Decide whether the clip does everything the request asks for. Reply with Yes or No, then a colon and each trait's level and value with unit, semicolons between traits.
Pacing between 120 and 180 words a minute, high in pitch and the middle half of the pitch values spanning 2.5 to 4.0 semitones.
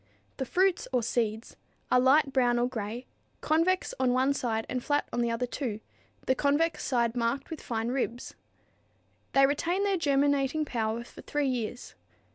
Yes: average, 165 wpm; very high, 255 Hz; average, 3.3 semitones